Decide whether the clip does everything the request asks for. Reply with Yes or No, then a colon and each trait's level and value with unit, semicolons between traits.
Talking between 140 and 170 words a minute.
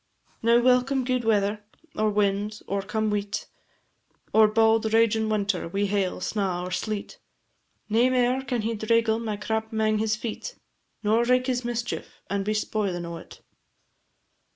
Yes: average, 150 wpm